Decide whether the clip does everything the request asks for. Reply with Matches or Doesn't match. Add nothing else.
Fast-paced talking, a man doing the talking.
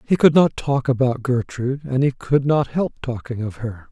Matches